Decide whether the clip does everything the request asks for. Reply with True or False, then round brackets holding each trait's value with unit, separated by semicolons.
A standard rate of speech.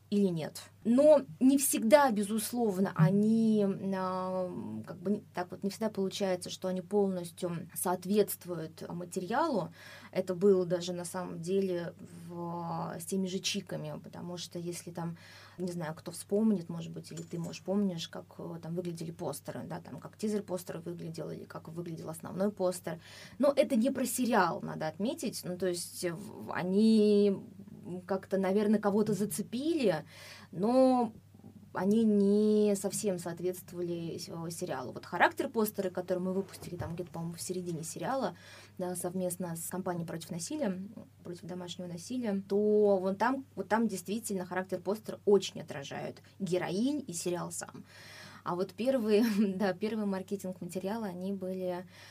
True (145 wpm)